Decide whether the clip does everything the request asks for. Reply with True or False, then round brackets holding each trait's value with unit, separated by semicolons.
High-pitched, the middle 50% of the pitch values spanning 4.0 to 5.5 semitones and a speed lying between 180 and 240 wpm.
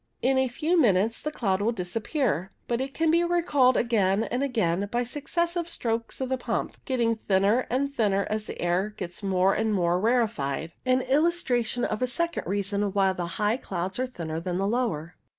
True (225 Hz; 5.2 semitones; 195 wpm)